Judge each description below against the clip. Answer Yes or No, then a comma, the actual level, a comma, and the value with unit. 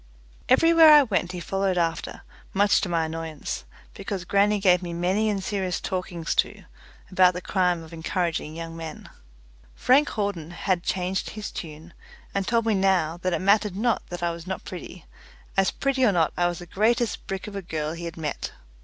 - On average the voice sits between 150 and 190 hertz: Yes, medium, 185 Hz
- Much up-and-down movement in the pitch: No, average, 3.2 semitones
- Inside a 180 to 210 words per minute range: Yes, average, 190 wpm